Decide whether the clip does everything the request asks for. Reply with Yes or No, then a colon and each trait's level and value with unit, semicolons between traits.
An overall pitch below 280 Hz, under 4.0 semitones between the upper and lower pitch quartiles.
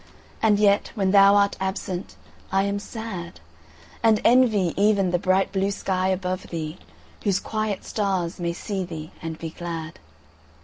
Yes: high, 190 Hz; narrow, 2.5 semitones